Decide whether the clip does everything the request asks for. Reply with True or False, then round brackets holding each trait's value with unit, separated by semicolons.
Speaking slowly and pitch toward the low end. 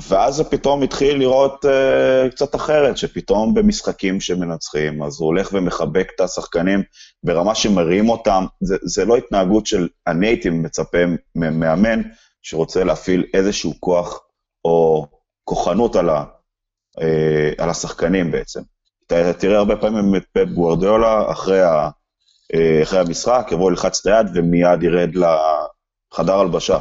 False (130 wpm; 90 Hz)